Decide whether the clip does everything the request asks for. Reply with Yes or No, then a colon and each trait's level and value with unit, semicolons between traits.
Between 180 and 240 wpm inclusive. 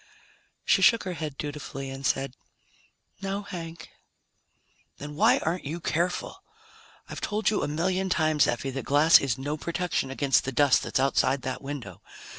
No: average, 165 wpm